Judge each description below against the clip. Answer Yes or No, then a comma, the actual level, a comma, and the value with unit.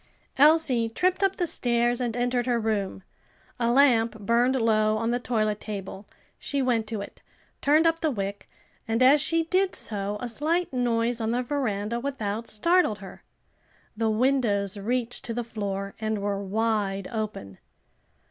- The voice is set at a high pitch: Yes, high, 230 Hz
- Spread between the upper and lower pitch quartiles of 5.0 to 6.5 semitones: No, average, 3.4 semitones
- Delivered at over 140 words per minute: Yes, average, 160 wpm